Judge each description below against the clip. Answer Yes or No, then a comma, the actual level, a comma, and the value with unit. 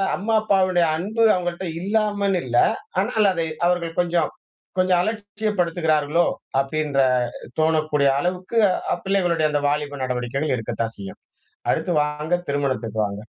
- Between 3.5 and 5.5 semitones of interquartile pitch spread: Yes, average, 4.5 semitones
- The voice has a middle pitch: Yes, medium, 170 Hz